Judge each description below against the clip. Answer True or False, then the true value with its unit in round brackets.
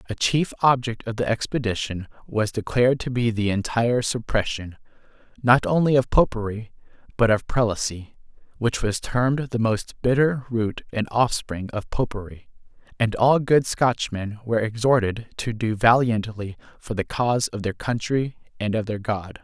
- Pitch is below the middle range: True (115 Hz)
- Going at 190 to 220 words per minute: False (155 wpm)